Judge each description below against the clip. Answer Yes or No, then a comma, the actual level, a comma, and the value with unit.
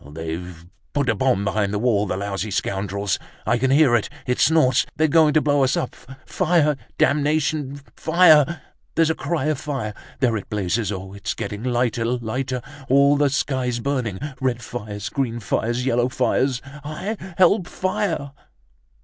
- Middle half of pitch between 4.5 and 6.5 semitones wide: Yes, wide, 5.5 semitones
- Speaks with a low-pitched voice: Yes, low, 125 Hz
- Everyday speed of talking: Yes, average, 160 wpm